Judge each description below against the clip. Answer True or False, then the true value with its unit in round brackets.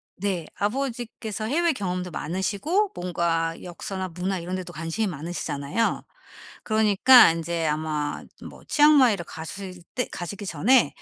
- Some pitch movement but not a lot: True (4.9 semitones)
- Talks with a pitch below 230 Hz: True (185 Hz)